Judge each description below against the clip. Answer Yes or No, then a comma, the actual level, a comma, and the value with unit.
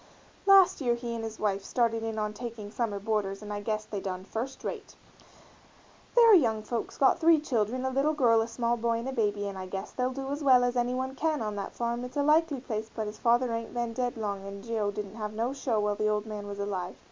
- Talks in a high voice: Yes, high, 230 Hz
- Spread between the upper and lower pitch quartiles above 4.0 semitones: No, average, 3.3 semitones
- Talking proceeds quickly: Yes, fast, 250 wpm